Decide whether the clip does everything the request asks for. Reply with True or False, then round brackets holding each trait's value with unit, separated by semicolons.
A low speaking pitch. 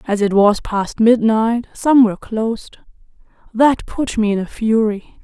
False (220 Hz)